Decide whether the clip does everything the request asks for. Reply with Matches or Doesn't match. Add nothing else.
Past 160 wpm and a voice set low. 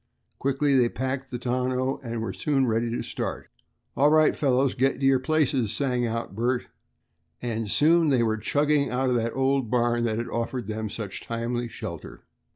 Matches